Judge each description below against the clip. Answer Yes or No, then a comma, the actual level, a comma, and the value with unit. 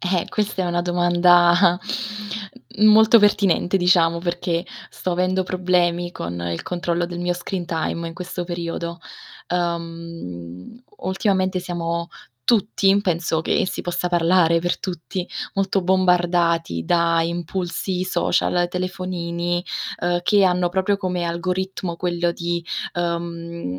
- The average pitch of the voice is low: No, medium, 175 Hz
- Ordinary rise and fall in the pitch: No, narrow, 1.4 semitones